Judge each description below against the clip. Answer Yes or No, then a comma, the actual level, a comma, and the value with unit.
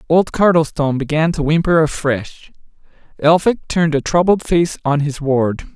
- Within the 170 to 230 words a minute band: No, average, 145 wpm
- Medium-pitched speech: Yes, medium, 155 Hz